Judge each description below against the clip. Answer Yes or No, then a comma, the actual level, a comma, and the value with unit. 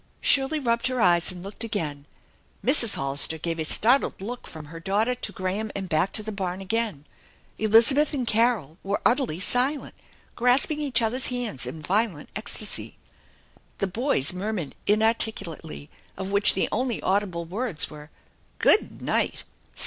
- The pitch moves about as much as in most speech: No, wide, 5.8 semitones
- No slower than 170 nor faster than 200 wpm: No, average, 155 wpm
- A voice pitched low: No, high, 205 Hz